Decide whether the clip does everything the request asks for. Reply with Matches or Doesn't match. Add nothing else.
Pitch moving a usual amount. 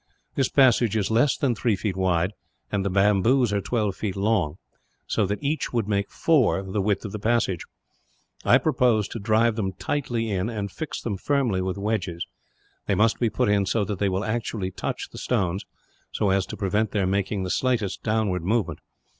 Matches